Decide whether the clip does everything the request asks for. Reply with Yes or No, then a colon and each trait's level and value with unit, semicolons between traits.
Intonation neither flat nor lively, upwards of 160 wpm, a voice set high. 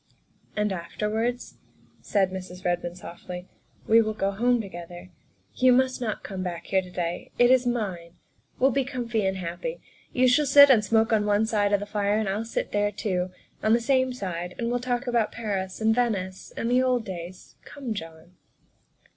Yes: average, 4.7 semitones; average, 190 wpm; high, 210 Hz